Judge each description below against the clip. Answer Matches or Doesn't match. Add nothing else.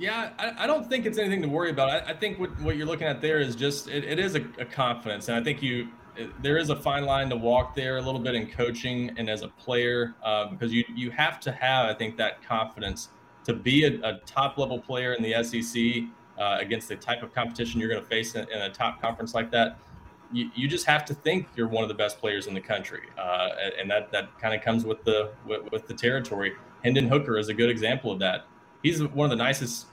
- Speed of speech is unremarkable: Doesn't match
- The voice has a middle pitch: Doesn't match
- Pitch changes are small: Doesn't match